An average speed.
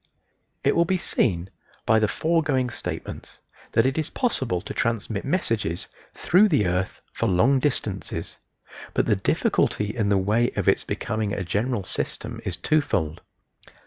Yes: average, 150 wpm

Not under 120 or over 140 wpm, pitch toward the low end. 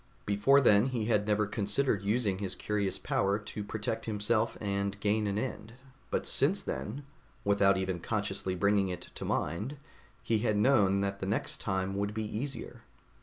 No: average, 170 wpm; low, 105 Hz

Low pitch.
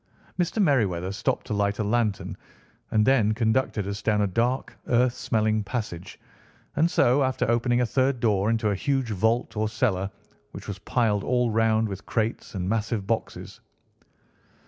Yes: low, 110 Hz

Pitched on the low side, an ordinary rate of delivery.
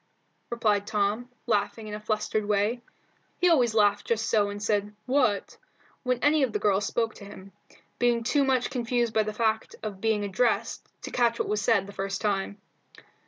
No: high, 215 Hz; average, 185 wpm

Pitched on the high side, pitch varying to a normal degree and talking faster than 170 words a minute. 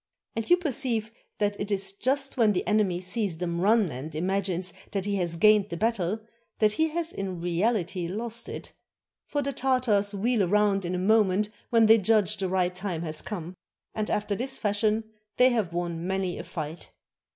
Yes: high, 205 Hz; average, 3.8 semitones; average, 185 wpm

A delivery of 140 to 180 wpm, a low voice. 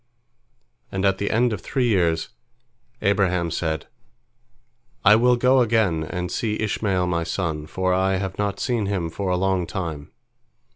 Yes: average, 155 wpm; very low, 95 Hz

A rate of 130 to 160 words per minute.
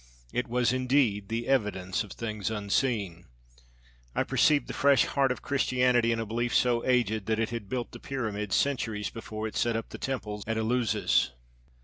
No: average, 180 wpm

